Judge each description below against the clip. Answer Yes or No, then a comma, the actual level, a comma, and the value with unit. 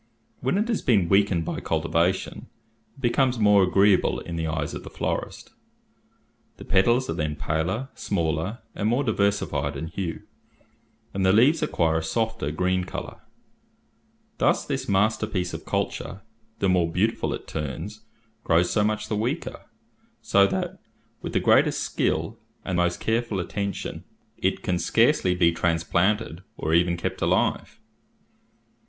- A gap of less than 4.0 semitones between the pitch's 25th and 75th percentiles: No, average, 4.5 semitones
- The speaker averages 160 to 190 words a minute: No, average, 145 wpm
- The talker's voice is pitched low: Yes, very low, 95 Hz